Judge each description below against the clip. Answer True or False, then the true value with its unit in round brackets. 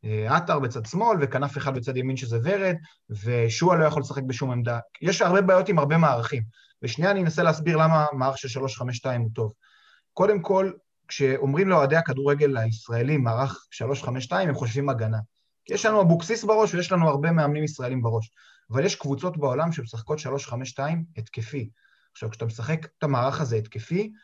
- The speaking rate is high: True (165 wpm)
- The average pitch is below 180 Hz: True (140 Hz)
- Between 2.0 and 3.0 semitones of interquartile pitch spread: False (5.4 semitones)